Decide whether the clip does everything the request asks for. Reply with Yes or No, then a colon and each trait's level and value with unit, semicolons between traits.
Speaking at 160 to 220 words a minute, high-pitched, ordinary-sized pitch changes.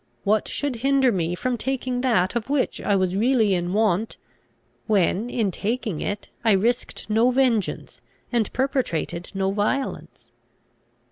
No: average, 140 wpm; high, 220 Hz; average, 4.6 semitones